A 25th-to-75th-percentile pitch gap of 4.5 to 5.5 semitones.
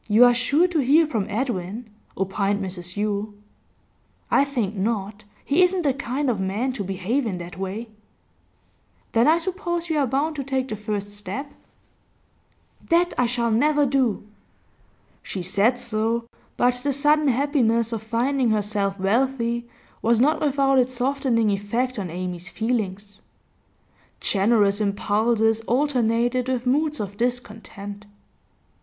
Yes: average, 4.8 semitones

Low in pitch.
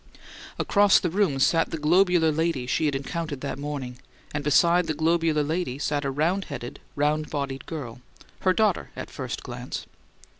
No: medium, 155 Hz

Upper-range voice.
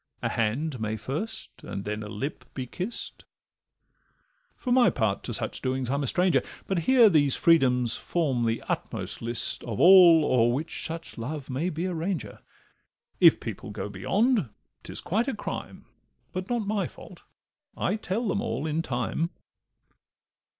No: medium, 155 Hz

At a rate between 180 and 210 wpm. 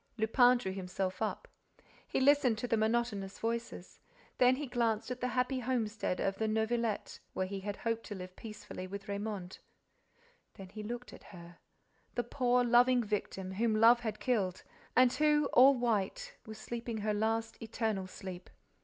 No: average, 165 wpm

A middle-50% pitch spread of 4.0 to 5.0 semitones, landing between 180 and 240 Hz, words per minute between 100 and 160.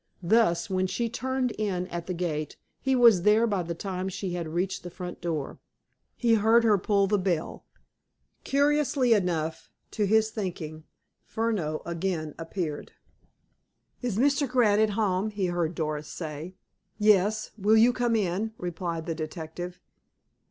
Yes: average, 4.4 semitones; high, 190 Hz; average, 150 wpm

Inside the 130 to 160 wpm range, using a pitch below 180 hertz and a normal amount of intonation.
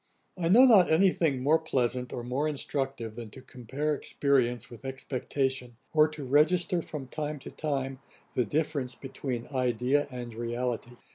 Yes: average, 155 wpm; low, 135 Hz; average, 3.5 semitones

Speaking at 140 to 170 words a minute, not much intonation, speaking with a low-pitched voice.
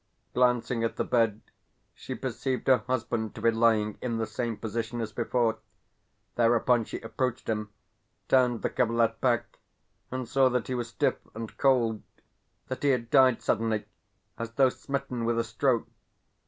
Yes: average, 160 wpm; narrow, 1.9 semitones; low, 115 Hz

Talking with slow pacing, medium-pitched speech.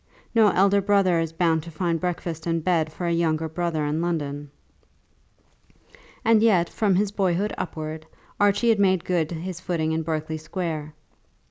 No: average, 160 wpm; medium, 170 Hz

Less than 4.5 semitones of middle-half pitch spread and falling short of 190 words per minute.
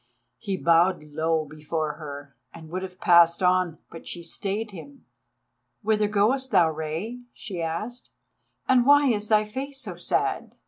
No: average, 5.0 semitones; average, 150 wpm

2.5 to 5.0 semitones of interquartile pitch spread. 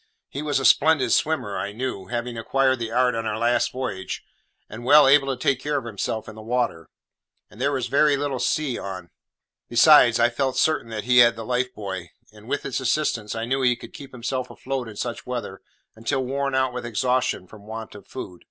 Yes: average, 3.1 semitones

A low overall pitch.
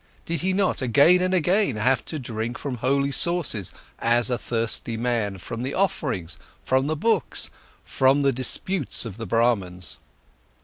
Yes: low, 130 Hz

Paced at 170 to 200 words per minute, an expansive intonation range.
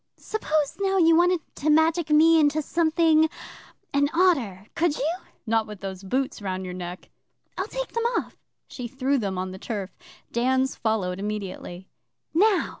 No: average, 160 wpm; wide, 8.4 semitones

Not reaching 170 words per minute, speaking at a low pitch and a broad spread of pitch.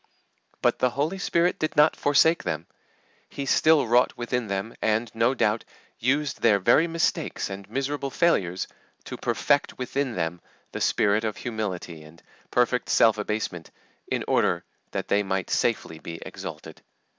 Yes: average, 150 wpm; low, 115 Hz; wide, 5.9 semitones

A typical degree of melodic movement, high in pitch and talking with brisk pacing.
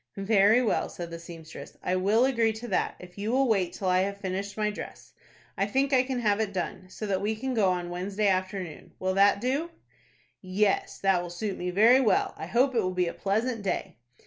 Yes: average, 3.2 semitones; high, 200 Hz; fast, 225 wpm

